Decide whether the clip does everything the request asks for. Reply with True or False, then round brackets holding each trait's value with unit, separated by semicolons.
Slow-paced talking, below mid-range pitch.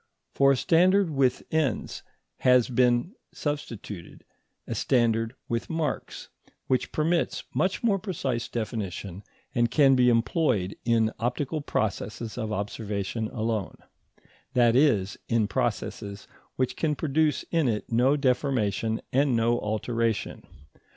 True (120 wpm; 120 Hz)